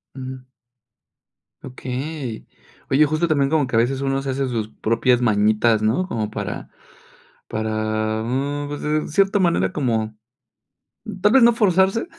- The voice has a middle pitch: No, low, 130 Hz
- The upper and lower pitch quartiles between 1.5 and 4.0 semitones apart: No, wide, 5.6 semitones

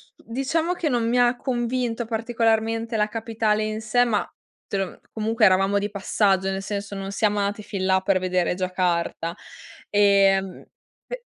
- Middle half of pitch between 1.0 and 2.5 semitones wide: No, average, 2.9 semitones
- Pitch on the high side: Yes, high, 210 Hz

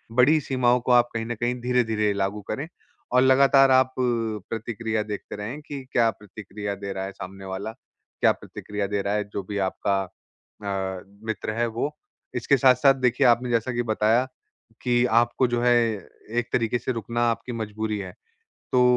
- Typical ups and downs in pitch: Yes, average, 3.2 semitones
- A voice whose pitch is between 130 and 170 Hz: No, low, 115 Hz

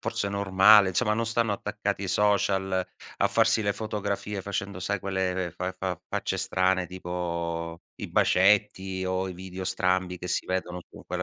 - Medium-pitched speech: No, very low, 95 Hz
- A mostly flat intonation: Yes, narrow, 1.7 semitones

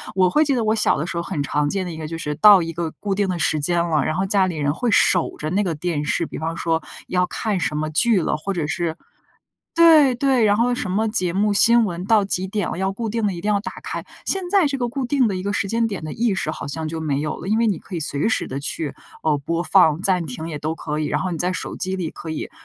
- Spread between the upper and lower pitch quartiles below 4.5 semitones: No, average, 4.9 semitones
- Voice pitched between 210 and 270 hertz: No, medium, 185 Hz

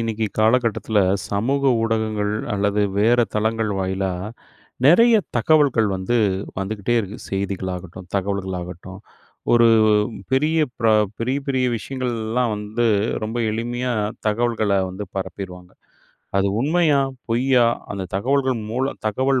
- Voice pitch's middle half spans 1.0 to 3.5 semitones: No, average, 4.0 semitones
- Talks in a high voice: No, low, 110 Hz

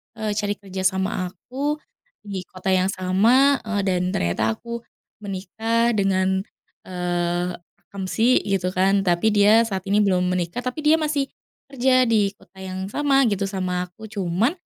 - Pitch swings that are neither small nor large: Yes, average, 3.7 semitones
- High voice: Yes, high, 195 Hz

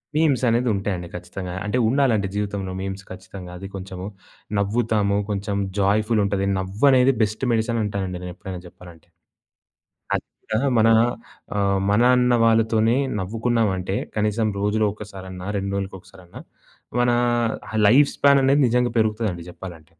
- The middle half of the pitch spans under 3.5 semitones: Yes, average, 3.1 semitones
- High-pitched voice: No, low, 100 Hz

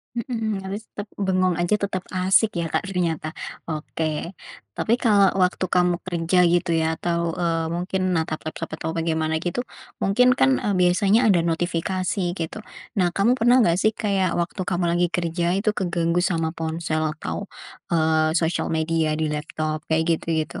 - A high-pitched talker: No, medium, 175 Hz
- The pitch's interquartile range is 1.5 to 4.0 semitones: Yes, average, 2.8 semitones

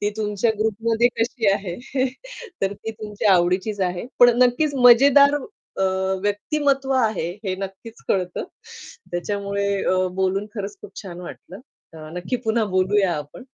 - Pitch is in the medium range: No, high, 205 Hz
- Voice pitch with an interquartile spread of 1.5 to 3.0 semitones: No, average, 3.5 semitones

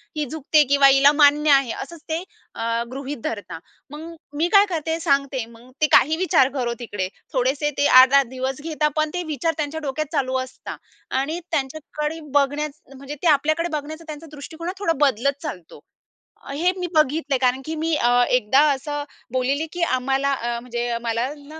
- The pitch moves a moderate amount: Yes, average, 3.2 semitones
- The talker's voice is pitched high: Yes, very high, 285 Hz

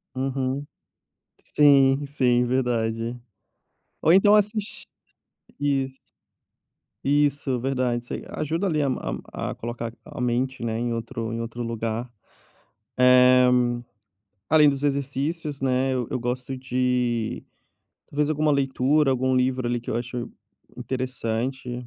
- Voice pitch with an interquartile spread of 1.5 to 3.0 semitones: Yes, narrow, 2.5 semitones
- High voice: No, low, 130 Hz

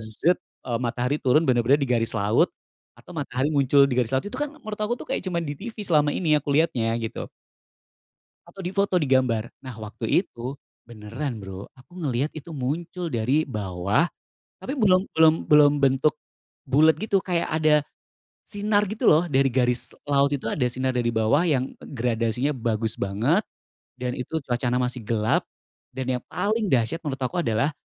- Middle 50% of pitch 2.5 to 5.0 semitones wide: No, wide, 5.4 semitones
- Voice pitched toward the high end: No, low, 135 Hz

